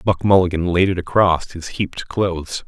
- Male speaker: Yes, male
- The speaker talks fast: No, average, 180 wpm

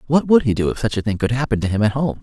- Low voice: Yes, low, 120 Hz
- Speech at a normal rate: No, fast, 380 wpm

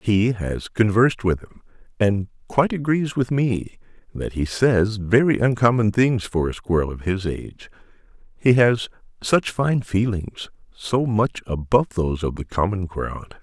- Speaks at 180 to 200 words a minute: No, average, 150 wpm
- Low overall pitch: Yes, low, 110 Hz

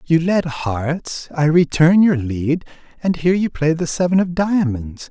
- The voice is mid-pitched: Yes, medium, 160 Hz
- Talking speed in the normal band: Yes, average, 175 wpm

